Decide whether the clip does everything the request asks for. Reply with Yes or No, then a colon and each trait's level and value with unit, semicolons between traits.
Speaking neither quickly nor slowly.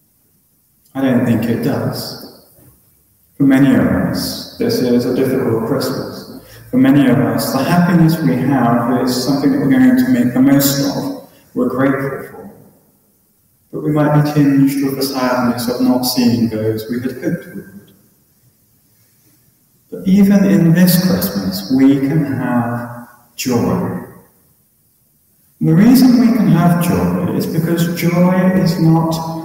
Yes: average, 145 wpm